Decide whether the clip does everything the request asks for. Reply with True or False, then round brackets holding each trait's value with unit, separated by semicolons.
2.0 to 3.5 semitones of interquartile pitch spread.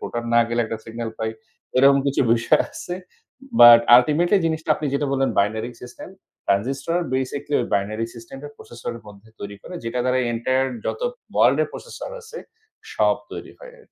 False (4.2 semitones)